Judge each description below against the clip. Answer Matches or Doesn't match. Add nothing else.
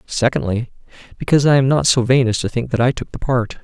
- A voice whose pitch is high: Doesn't match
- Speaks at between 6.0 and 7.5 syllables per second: Matches